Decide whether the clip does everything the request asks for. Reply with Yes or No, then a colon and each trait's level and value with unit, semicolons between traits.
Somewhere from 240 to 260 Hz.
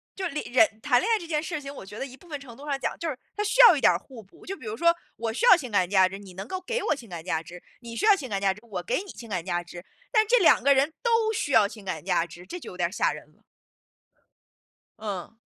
Yes: very high, 250 Hz